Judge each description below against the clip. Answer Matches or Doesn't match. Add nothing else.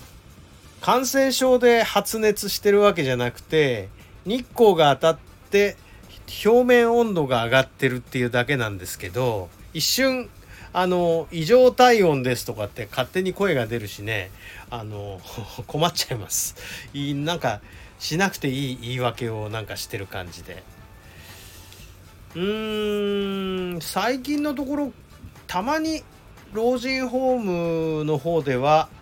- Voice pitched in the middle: Matches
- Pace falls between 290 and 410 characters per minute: Doesn't match